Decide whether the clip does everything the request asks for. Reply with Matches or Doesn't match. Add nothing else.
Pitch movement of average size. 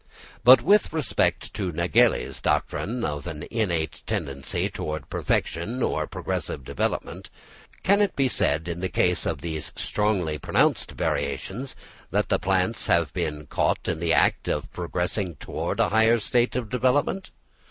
Doesn't match